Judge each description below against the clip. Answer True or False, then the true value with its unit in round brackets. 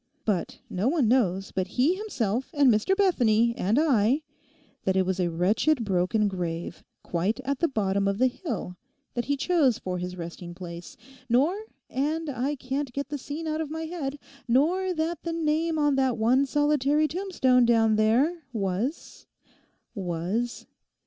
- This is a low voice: False (255 Hz)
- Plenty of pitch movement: True (7.1 semitones)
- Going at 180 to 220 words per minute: False (155 wpm)